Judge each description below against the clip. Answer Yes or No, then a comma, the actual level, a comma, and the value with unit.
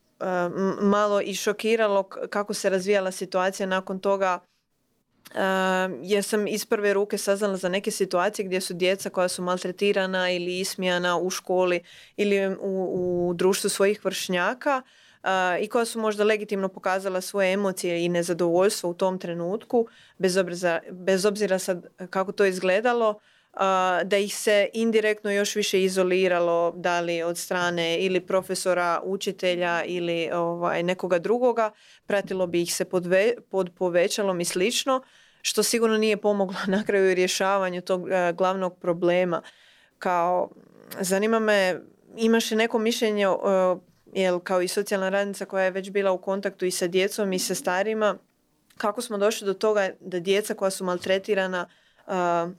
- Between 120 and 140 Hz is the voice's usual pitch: No, high, 190 Hz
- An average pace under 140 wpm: No, average, 145 wpm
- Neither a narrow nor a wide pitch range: No, narrow, 2.2 semitones